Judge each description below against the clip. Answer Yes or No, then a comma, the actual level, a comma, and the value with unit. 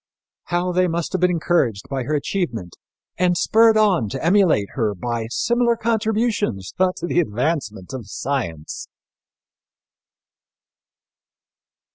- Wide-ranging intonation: Yes, wide, 8.2 semitones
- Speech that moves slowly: Yes, slow, 115 wpm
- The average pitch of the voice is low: No, medium, 170 Hz